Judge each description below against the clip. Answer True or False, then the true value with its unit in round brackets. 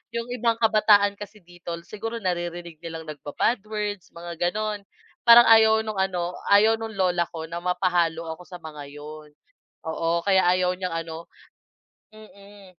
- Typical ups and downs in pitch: True (3.9 semitones)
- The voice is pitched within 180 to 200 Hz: True (185 Hz)